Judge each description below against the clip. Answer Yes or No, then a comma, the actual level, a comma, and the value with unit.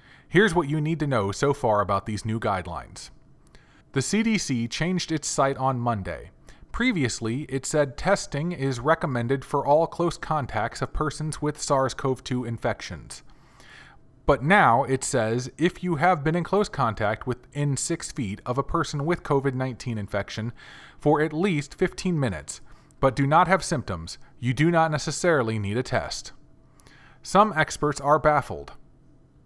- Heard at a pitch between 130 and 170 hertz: Yes, medium, 140 Hz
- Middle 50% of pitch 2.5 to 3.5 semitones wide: No, average, 4.7 semitones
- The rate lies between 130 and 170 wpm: Yes, average, 155 wpm